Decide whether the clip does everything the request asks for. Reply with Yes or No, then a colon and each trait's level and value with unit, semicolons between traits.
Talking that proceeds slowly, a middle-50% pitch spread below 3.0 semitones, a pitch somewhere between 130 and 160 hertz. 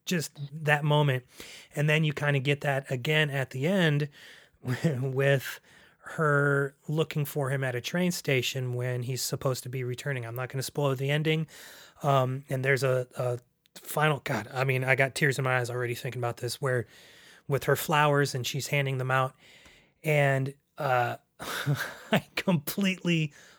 No: average, 170 wpm; narrow, 2.5 semitones; medium, 140 Hz